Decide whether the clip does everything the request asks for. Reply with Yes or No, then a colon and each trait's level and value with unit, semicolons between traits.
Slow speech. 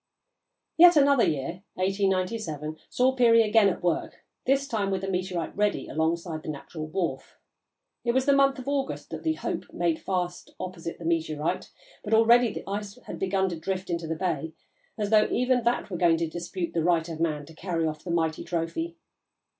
No: average, 190 wpm